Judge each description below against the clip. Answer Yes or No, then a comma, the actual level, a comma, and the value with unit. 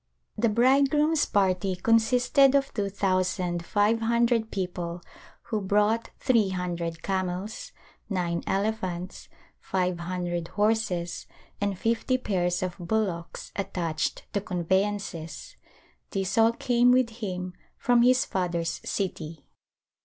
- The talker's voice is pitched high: Yes, high, 195 Hz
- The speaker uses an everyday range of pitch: Yes, average, 4.2 semitones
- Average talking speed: No, slow, 110 wpm